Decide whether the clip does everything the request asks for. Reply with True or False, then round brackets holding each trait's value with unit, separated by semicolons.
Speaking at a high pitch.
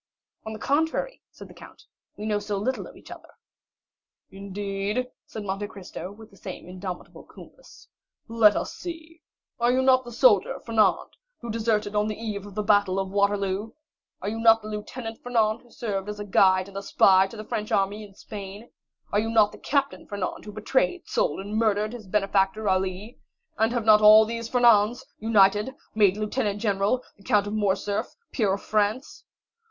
True (210 Hz)